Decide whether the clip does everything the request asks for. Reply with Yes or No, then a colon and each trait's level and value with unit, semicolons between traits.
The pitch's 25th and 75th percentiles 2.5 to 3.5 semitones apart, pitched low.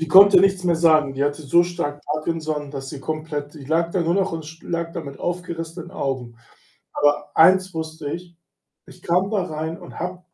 No: average, 2.9 semitones; medium, 160 Hz